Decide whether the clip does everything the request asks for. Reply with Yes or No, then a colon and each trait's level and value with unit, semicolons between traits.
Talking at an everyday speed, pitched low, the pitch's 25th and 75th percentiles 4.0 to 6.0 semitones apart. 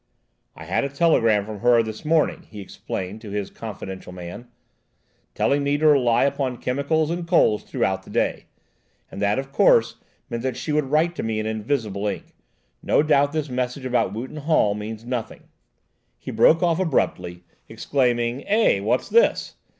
Yes: average, 170 wpm; low, 125 Hz; average, 5.3 semitones